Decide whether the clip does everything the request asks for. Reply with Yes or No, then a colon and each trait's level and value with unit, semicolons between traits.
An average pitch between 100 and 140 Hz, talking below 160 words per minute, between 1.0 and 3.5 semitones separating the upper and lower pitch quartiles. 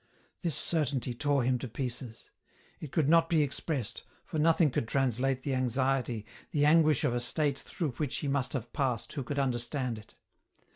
No: low, 135 Hz; average, 180 wpm; average, 3.1 semitones